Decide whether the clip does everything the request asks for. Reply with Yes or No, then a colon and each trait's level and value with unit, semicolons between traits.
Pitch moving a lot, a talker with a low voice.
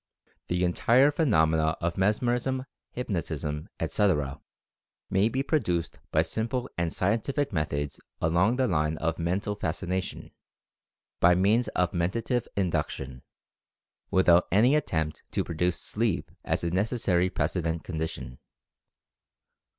Yes: wide, 5.7 semitones; very low, 90 Hz